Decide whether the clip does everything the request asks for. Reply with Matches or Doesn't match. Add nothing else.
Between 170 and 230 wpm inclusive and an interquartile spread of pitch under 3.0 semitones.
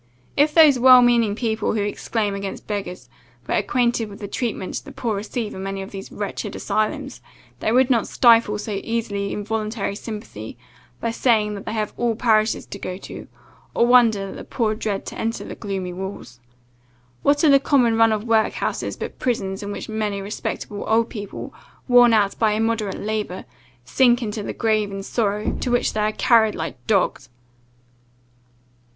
Matches